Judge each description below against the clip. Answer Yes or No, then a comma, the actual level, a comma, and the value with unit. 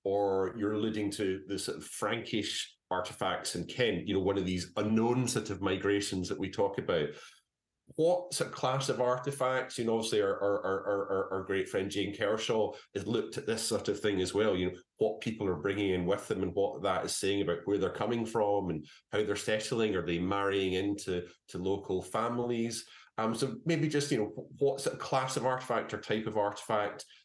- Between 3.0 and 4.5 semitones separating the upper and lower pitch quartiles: Yes, average, 3.4 semitones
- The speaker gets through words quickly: Yes, fast, 215 wpm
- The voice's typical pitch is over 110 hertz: No, low, 105 Hz